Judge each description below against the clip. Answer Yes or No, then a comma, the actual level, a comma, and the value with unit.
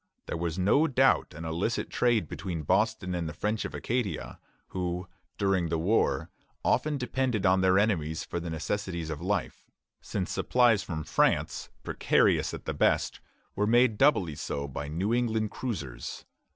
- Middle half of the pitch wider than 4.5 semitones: Yes, average, 5.2 semitones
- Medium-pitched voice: No, very low, 95 Hz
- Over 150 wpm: Yes, average, 160 wpm